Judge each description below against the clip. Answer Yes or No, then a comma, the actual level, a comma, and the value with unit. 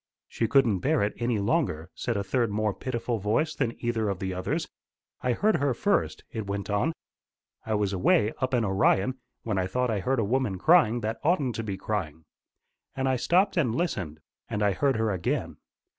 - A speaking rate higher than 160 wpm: Yes, average, 200 wpm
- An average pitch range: Yes, average, 4.6 semitones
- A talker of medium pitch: No, low, 115 Hz